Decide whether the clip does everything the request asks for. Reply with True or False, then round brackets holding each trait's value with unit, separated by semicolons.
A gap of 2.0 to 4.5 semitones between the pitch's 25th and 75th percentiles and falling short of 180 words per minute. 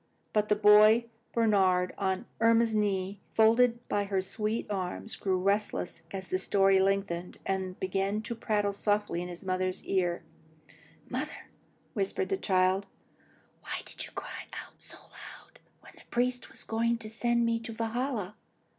True (3.1 semitones; 155 wpm)